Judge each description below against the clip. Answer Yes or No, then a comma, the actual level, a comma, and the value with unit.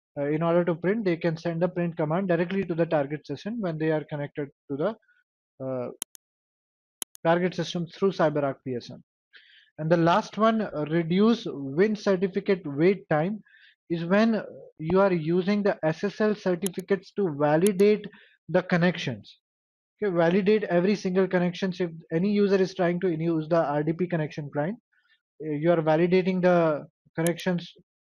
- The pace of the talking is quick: No, average, 150 wpm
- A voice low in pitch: No, medium, 175 Hz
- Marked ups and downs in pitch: No, average, 3.8 semitones